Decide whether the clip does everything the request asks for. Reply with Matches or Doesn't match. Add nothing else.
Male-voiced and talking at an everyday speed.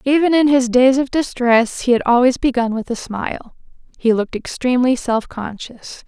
Doesn't match